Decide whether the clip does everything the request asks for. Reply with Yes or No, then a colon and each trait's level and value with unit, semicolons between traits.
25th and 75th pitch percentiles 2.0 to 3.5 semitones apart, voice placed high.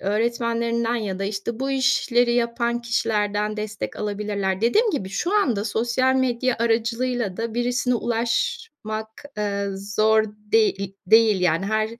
Yes: narrow, 2.5 semitones; high, 225 Hz